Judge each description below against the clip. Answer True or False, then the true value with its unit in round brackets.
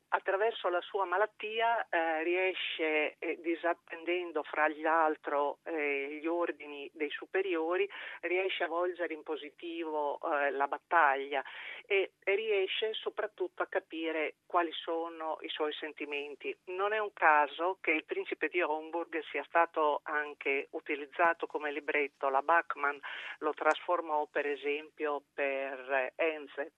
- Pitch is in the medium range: True (160 Hz)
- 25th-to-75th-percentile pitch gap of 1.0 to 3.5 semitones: True (3.0 semitones)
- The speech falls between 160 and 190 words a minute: False (130 wpm)